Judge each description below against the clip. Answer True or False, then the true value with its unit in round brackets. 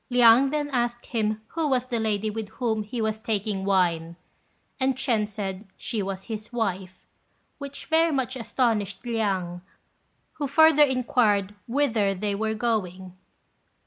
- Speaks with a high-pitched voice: True (220 Hz)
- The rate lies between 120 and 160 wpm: True (145 wpm)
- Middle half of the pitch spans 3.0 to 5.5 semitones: True (4.0 semitones)